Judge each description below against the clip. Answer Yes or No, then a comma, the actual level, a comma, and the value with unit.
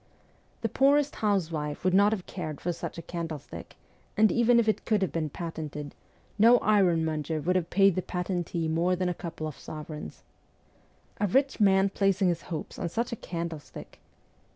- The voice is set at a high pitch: No, medium, 180 Hz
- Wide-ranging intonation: No, average, 4.0 semitones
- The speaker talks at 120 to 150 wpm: No, average, 175 wpm